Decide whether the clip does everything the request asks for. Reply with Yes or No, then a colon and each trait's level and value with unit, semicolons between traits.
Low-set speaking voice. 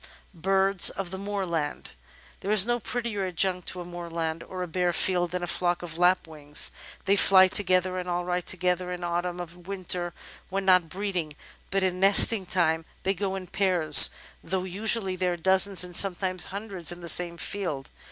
No: medium, 180 Hz